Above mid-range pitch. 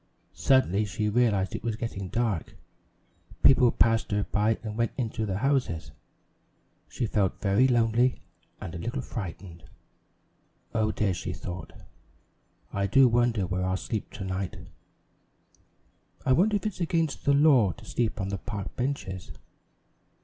No: low, 110 Hz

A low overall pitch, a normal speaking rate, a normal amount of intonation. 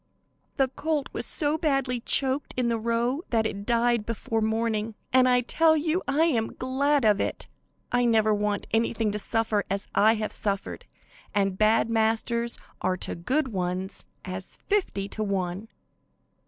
No: high, 225 Hz; average, 160 wpm; average, 3.7 semitones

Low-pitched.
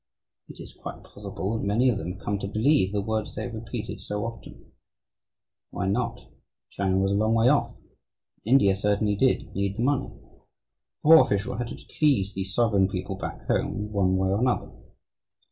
Yes: low, 105 Hz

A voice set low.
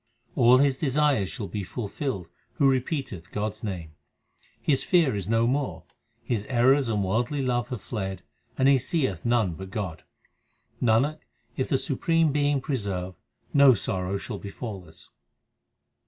Yes: low, 120 Hz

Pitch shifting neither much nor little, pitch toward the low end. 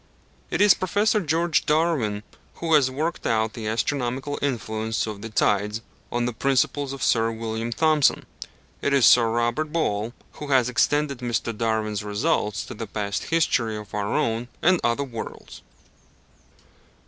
Yes: average, 4.6 semitones; low, 120 Hz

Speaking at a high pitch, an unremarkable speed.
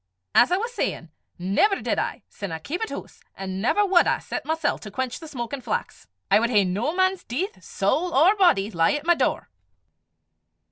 Yes: very high, 290 Hz; average, 195 wpm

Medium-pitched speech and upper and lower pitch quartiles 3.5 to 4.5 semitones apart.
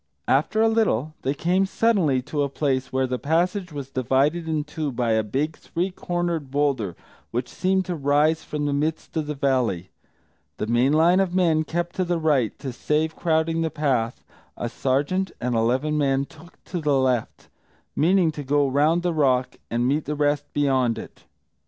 Yes: medium, 150 Hz; average, 3.9 semitones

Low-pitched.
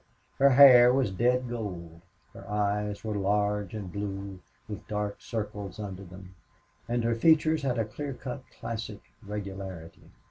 Yes: low, 105 Hz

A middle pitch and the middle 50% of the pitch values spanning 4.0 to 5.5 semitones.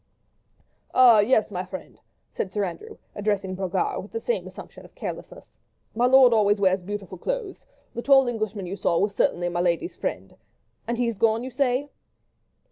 No: high, 215 Hz; average, 5.0 semitones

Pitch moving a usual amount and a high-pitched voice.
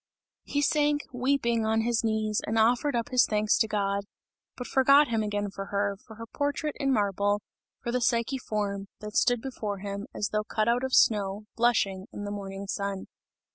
Yes: average, 3.3 semitones; high, 220 Hz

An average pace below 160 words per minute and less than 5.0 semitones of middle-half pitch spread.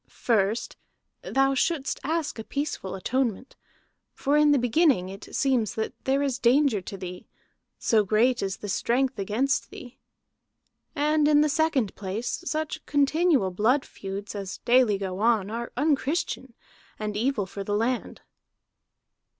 No: average, 140 wpm; wide, 5.5 semitones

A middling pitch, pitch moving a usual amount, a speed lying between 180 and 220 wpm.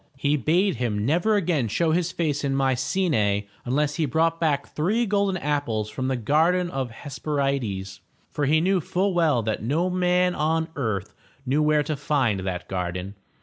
No: medium, 145 Hz; wide, 5.9 semitones; average, 185 wpm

